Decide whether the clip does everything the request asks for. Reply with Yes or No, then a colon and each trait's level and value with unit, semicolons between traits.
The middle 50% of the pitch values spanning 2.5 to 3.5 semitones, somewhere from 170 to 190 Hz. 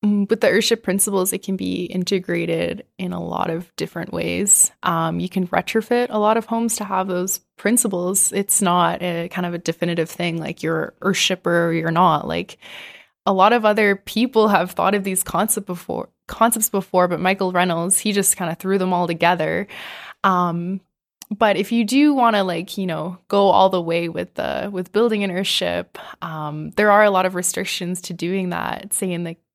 Yes: average, 2.9 semitones; medium, 185 Hz